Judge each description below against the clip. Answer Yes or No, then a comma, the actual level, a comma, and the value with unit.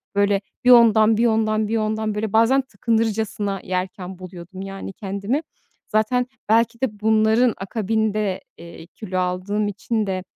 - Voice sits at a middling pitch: No, high, 215 Hz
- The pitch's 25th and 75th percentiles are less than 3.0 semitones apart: Yes, narrow, 2.4 semitones